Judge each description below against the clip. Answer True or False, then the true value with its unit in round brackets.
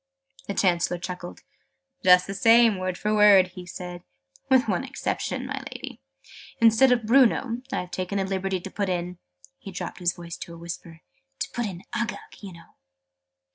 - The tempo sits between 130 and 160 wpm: False (175 wpm)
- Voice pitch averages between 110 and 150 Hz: False (185 Hz)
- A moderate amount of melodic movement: True (3.3 semitones)